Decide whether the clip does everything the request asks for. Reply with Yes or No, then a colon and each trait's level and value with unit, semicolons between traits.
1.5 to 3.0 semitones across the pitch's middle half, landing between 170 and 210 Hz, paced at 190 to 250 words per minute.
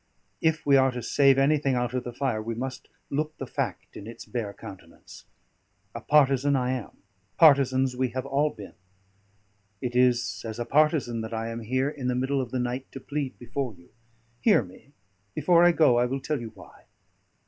No: narrow, 2.6 semitones; low, 130 Hz; average, 195 wpm